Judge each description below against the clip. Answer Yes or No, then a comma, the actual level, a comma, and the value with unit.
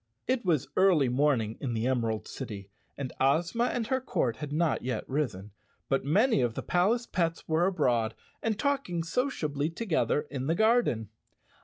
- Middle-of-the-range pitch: Yes, medium, 150 Hz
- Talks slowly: No, average, 170 wpm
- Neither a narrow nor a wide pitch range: No, wide, 7.7 semitones